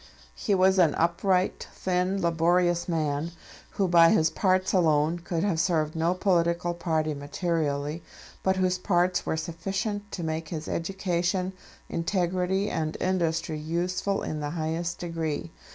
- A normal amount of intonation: No, narrow, 2.3 semitones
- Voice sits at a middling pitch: Yes, medium, 170 Hz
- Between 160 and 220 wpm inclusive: No, slow, 135 wpm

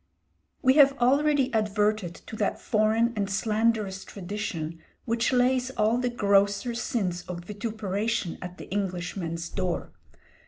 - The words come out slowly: Yes, slow, 125 wpm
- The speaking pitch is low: No, high, 210 Hz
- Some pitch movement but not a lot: Yes, average, 3.8 semitones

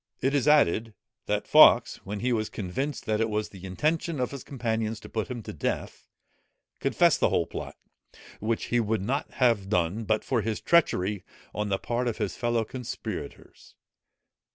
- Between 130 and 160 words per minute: No, average, 175 wpm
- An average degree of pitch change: Yes, average, 3.1 semitones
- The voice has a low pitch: Yes, low, 115 Hz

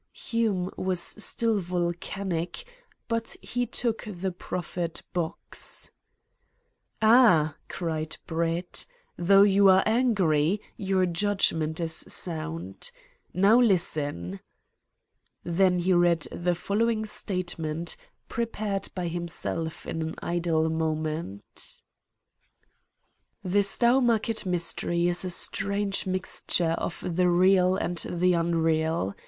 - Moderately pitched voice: Yes, medium, 180 Hz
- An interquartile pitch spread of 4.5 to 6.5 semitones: No, average, 3.3 semitones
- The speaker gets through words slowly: Yes, slow, 100 wpm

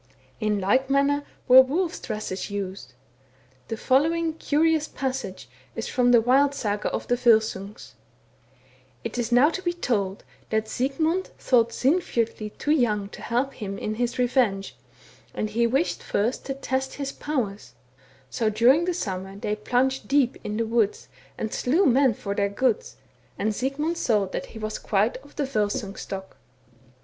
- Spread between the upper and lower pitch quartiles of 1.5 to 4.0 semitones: No, average, 4.6 semitones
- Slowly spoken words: No, average, 165 wpm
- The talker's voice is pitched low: No, high, 240 Hz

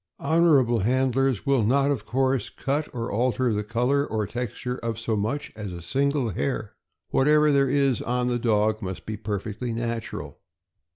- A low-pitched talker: Yes, low, 120 Hz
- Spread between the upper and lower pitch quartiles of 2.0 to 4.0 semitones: Yes, average, 3.7 semitones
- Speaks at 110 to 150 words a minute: No, average, 165 wpm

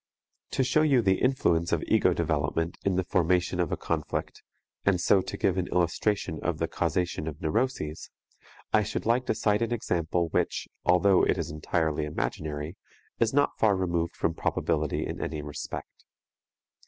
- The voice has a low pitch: Yes, very low, 90 Hz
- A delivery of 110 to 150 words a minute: No, average, 165 wpm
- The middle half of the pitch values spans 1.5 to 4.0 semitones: No, average, 4.5 semitones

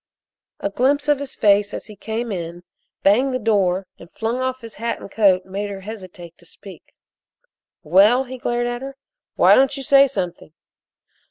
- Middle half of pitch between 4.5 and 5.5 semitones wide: Yes, average, 5.0 semitones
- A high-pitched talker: Yes, high, 220 Hz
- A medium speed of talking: Yes, average, 180 wpm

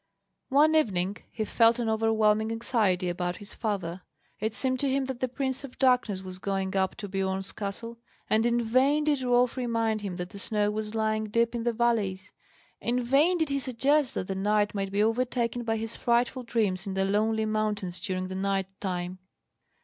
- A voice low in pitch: No, high, 220 Hz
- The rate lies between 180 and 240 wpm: Yes, average, 195 wpm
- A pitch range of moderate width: Yes, average, 3.8 semitones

